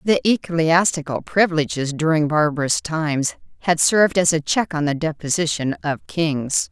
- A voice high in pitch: No, medium, 160 Hz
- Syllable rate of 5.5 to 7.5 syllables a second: No, 4.9 syllables/s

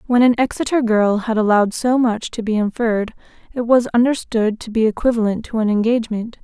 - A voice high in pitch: Yes, high, 230 Hz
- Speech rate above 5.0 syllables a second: Yes, 5.8 syllables/s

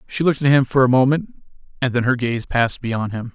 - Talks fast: Yes, fast, 250 wpm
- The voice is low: Yes, low, 130 Hz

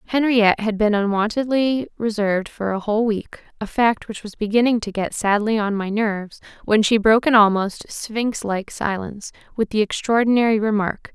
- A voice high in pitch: Yes, high, 215 Hz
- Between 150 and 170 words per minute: Yes, average, 165 wpm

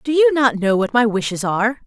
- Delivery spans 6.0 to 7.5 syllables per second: No, 5.8 syllables/s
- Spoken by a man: No, female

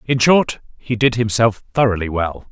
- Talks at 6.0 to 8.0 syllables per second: No, 4.7 syllables/s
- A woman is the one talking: No, male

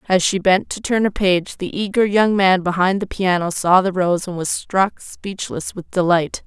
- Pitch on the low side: No, high, 190 Hz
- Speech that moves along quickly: Yes, fast, 215 wpm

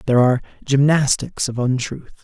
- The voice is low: Yes, low, 130 Hz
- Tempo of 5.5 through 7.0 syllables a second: Yes, 5.7 syllables/s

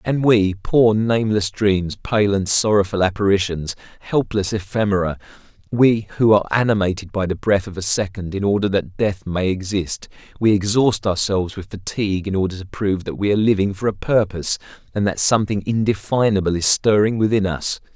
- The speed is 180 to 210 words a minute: No, average, 170 wpm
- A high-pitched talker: No, low, 100 Hz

